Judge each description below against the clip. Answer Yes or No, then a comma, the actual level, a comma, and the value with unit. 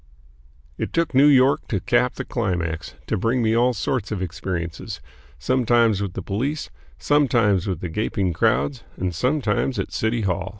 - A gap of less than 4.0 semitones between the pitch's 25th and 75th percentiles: No, wide, 5.6 semitones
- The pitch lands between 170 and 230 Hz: No, low, 105 Hz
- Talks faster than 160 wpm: Yes, average, 170 wpm